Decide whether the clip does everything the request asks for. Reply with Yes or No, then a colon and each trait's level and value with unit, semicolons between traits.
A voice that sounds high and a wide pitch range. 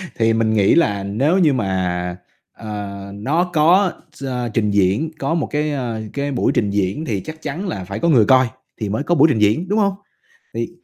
No: low, 115 Hz; wide, 7.5 semitones